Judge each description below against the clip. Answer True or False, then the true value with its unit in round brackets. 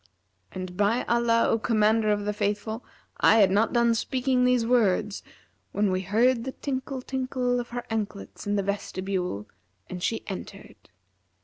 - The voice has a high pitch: True (220 Hz)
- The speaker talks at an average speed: True (155 wpm)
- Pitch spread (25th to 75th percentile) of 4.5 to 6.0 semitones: False (3.3 semitones)